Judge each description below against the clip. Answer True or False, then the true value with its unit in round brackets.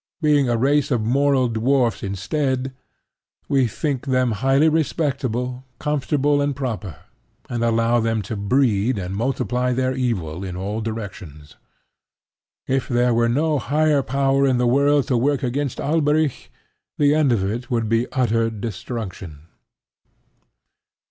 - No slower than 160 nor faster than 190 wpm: False (135 wpm)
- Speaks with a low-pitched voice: True (125 Hz)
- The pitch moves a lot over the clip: False (3.7 semitones)